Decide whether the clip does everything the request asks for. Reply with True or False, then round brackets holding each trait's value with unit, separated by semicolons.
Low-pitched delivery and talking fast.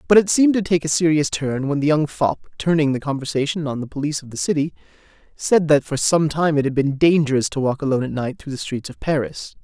False (150 Hz; 250 wpm)